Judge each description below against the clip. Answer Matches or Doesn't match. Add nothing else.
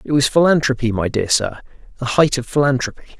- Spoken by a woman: Doesn't match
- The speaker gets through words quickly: Doesn't match